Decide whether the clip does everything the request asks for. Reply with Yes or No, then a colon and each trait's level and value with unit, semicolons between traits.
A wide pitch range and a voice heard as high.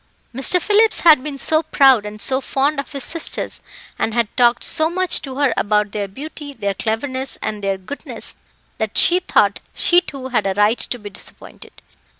Yes: wide, 6.1 semitones; very high, 265 Hz